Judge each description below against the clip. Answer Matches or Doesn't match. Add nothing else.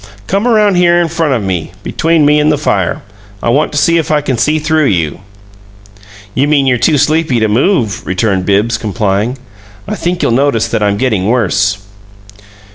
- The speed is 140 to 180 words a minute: Doesn't match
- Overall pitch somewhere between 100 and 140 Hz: Matches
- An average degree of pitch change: Doesn't match